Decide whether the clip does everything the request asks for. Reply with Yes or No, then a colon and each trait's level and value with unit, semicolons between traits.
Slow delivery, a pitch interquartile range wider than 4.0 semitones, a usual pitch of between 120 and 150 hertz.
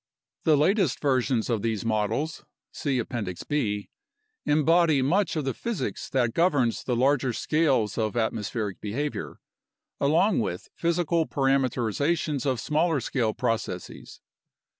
Yes: slow, 125 wpm; average, 5.3 semitones; low, 135 Hz